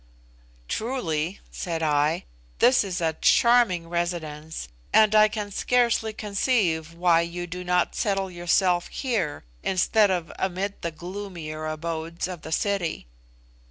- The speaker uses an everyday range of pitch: Yes, average, 3.7 semitones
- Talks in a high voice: No, medium, 180 Hz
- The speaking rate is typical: No, slow, 125 wpm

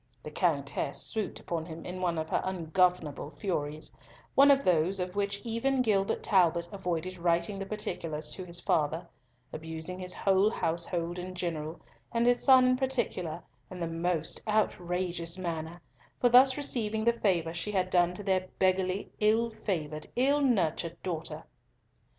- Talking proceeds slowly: No, average, 150 wpm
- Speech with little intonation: No, average, 4.0 semitones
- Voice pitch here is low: No, medium, 180 Hz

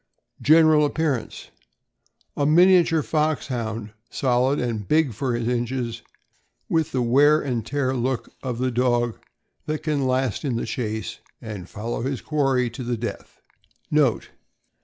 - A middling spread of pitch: Yes, average, 3.9 semitones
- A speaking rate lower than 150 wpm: Yes, average, 140 wpm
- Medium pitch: No, low, 130 Hz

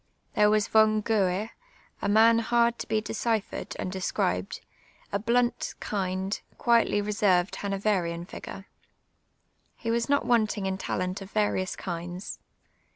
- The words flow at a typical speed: No, slow, 130 wpm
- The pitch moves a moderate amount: Yes, average, 3.0 semitones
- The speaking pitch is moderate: No, high, 205 Hz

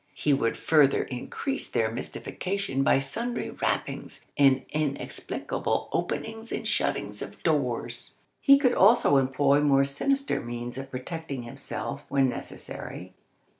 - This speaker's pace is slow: Yes, slow, 125 wpm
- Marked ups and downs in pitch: Yes, wide, 7.0 semitones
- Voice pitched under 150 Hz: Yes, medium, 140 Hz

